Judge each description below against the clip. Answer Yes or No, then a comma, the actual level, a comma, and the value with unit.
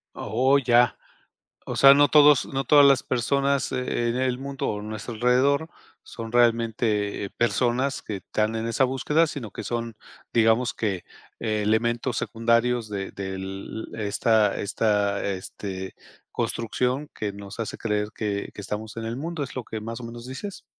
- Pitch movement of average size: Yes, average, 3.5 semitones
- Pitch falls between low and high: No, low, 115 Hz